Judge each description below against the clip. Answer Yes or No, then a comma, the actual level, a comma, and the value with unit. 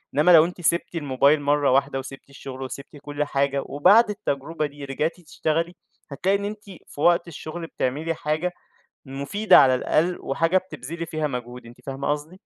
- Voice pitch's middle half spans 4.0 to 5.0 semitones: No, average, 3.4 semitones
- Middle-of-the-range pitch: Yes, medium, 150 Hz